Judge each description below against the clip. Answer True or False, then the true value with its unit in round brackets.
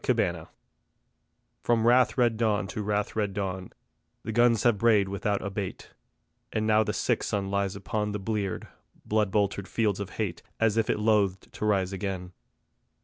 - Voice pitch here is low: True (105 Hz)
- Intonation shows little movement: True (2.0 semitones)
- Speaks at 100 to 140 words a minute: False (170 wpm)